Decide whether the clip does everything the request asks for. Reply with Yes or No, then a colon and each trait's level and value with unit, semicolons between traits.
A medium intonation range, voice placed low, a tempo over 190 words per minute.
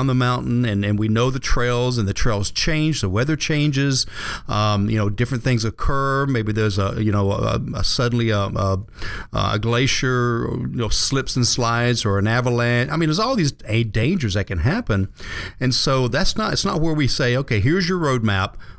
Yes: average, 4.1 semitones; low, 120 Hz; average, 200 wpm